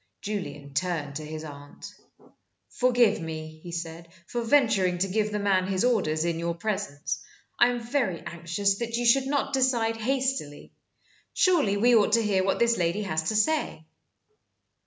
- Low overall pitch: No, high, 200 Hz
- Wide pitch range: Yes, wide, 5.9 semitones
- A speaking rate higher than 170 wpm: No, average, 165 wpm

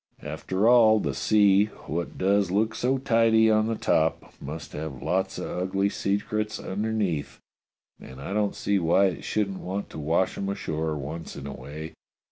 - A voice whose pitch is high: No, very low, 95 Hz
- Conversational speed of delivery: Yes, average, 170 wpm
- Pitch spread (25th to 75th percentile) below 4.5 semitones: No, average, 5.3 semitones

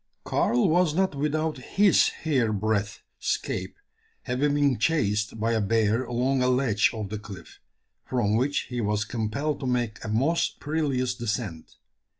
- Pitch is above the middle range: No, low, 125 Hz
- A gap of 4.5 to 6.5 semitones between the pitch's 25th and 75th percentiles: Yes, average, 4.9 semitones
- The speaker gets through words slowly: No, average, 150 wpm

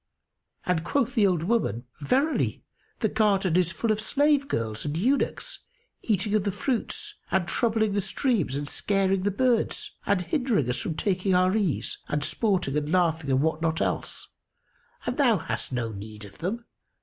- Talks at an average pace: Yes, average, 175 wpm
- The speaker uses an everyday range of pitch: No, wide, 6.0 semitones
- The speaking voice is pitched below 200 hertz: Yes, high, 190 Hz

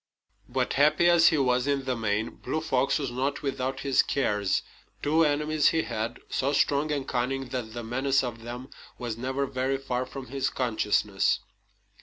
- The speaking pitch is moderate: No, low, 130 Hz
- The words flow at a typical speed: Yes, average, 175 wpm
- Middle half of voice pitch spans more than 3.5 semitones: No, narrow, 2.5 semitones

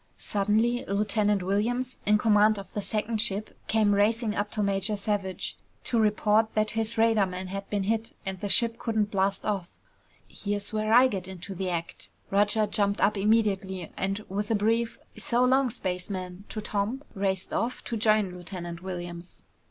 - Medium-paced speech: Yes, average, 165 wpm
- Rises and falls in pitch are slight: Yes, narrow, 2.2 semitones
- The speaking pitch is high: Yes, high, 205 Hz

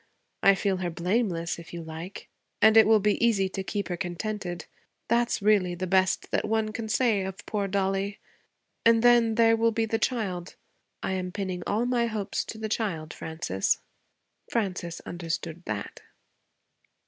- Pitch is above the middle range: Yes, high, 200 Hz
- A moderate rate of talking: Yes, average, 170 wpm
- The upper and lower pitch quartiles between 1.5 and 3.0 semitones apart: No, average, 3.8 semitones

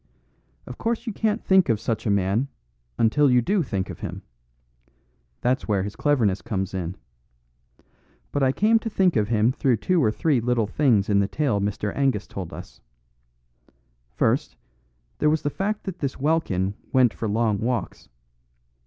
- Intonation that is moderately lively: No, wide, 6.6 semitones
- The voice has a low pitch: Yes, low, 120 Hz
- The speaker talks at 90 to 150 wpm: No, average, 170 wpm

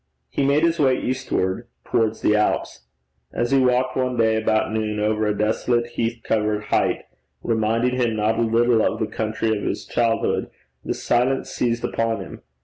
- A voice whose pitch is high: No, low, 115 Hz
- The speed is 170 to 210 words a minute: Yes, average, 175 wpm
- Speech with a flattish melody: Yes, narrow, 2.2 semitones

